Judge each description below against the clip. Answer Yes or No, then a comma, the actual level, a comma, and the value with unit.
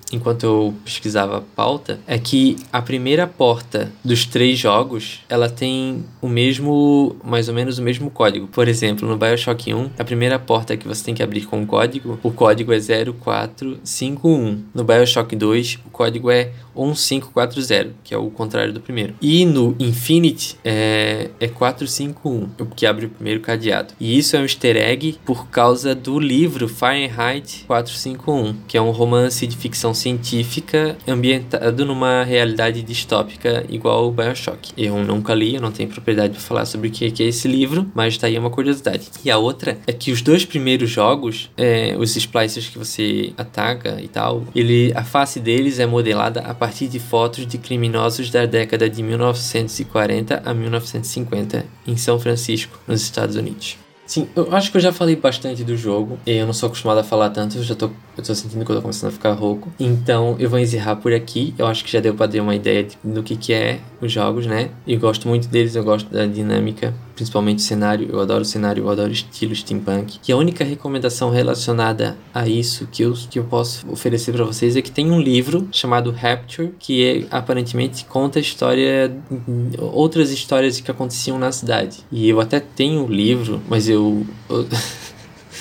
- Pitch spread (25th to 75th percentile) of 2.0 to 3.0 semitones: Yes, narrow, 2.5 semitones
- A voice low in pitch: Yes, low, 120 Hz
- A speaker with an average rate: No, fast, 190 wpm